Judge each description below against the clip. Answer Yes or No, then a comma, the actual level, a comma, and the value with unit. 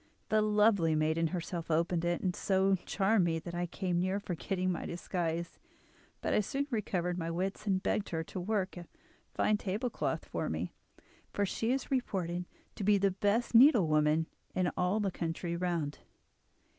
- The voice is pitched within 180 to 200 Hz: Yes, medium, 185 Hz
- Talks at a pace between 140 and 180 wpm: Yes, average, 170 wpm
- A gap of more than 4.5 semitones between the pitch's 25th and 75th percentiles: No, average, 3.2 semitones